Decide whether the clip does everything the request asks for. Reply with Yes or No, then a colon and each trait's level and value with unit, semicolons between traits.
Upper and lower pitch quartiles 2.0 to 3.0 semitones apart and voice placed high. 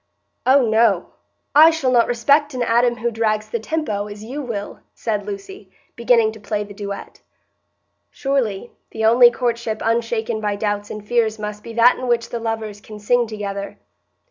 Yes: narrow, 2.4 semitones; high, 225 Hz